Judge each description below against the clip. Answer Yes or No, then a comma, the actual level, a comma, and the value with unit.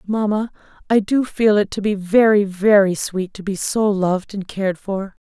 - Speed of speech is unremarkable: Yes, average, 195 wpm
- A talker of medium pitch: No, high, 200 Hz